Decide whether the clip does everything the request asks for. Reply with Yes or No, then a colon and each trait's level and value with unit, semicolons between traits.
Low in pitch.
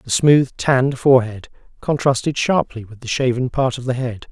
Yes: low, 125 Hz